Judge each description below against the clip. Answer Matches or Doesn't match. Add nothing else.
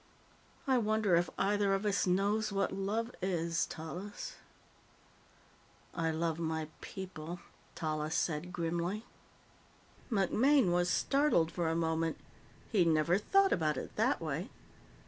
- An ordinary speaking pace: Doesn't match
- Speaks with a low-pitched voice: Doesn't match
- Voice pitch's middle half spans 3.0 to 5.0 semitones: Matches